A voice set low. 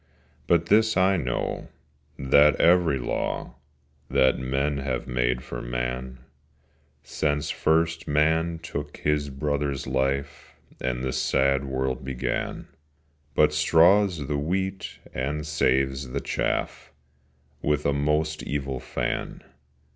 Yes: very low, 70 Hz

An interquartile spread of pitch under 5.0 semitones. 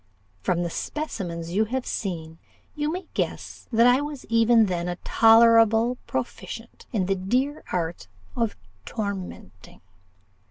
No: average, 5.3 semitones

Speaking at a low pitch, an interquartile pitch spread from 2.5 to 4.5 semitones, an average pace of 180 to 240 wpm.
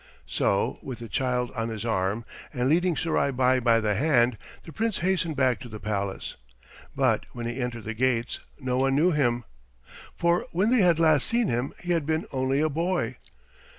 No: low, 130 Hz; wide, 5.6 semitones; average, 190 wpm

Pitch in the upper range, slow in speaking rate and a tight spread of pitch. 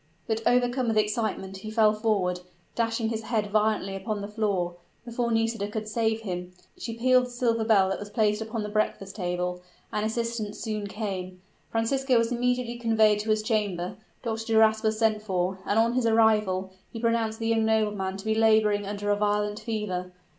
No: high, 215 Hz; average, 185 wpm; narrow, 1.8 semitones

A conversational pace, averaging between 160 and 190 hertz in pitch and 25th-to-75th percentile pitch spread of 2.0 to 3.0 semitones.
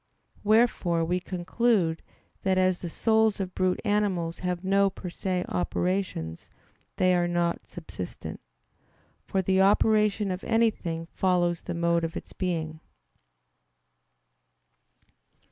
No: slow, 115 wpm; medium, 185 Hz; narrow, 2.5 semitones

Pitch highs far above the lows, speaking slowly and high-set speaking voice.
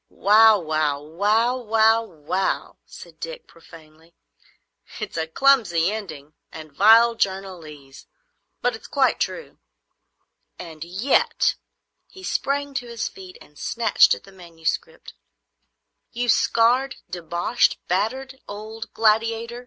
Yes: wide, 6.0 semitones; slow, 95 wpm; high, 210 Hz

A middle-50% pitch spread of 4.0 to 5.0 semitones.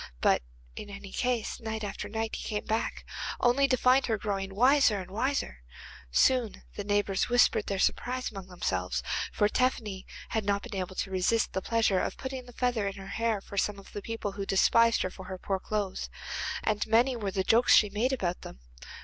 No: average, 3.3 semitones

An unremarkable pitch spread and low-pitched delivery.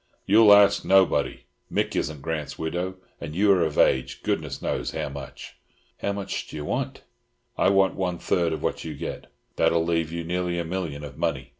Yes: average, 3.5 semitones; very low, 85 Hz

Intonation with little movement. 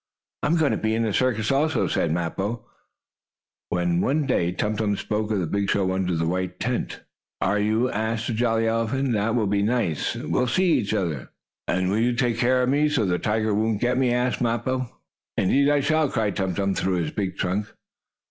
No: average, 4.2 semitones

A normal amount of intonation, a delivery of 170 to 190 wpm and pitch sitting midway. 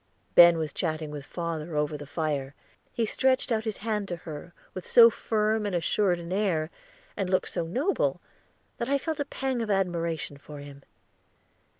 No: wide, 5.7 semitones; average, 180 wpm; medium, 175 Hz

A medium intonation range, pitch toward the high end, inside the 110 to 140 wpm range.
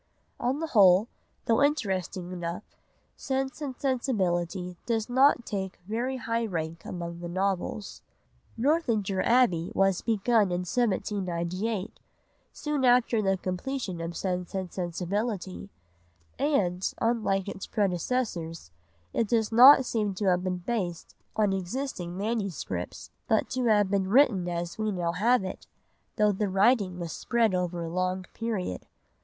Yes: average, 4.5 semitones; high, 195 Hz; slow, 135 wpm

